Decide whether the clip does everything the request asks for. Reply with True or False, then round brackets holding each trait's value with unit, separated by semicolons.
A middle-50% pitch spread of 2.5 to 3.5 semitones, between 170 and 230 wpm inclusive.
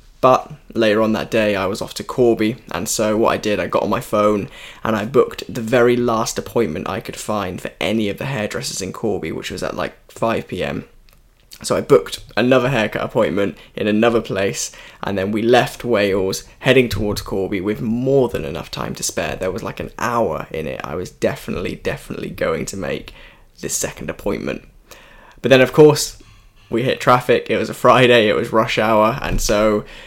True (2.8 semitones; 200 wpm)